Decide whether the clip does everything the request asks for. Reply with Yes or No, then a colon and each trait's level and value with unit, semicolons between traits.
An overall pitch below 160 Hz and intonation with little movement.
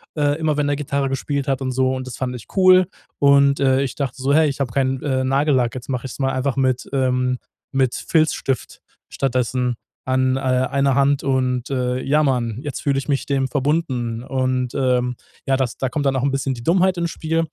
Yes: low, 135 Hz; narrow, 1.7 semitones